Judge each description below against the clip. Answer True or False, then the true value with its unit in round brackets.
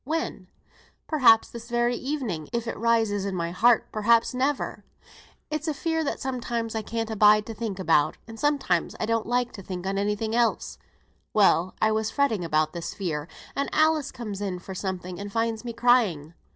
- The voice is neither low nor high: False (225 Hz)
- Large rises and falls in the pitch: False (3.8 semitones)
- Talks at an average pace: True (190 wpm)